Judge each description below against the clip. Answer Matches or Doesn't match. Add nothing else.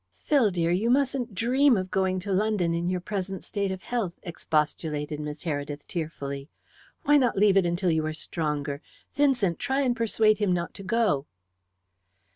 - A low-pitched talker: Doesn't match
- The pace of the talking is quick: Doesn't match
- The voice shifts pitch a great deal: Matches